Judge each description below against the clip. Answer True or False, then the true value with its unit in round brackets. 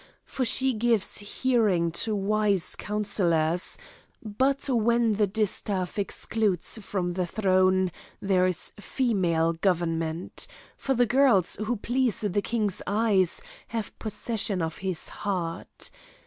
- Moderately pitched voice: False (205 Hz)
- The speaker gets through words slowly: True (120 wpm)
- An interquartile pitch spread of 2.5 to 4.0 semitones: True (3.7 semitones)